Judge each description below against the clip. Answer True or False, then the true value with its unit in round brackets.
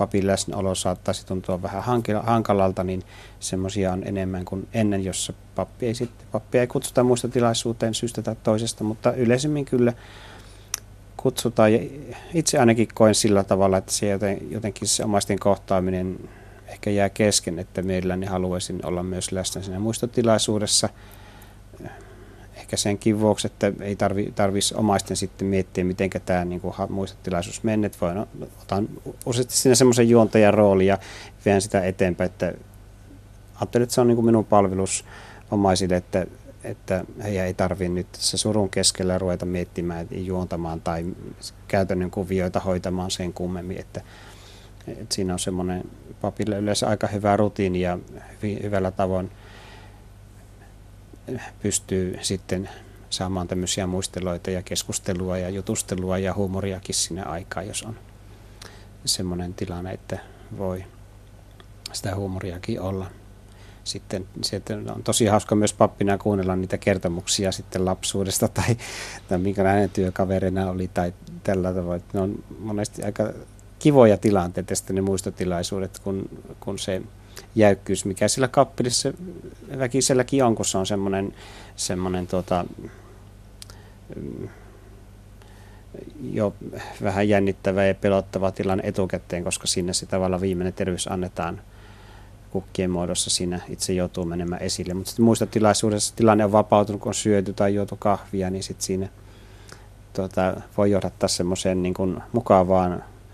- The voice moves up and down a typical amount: False (2.0 semitones)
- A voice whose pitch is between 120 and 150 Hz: False (100 Hz)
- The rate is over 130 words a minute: False (125 wpm)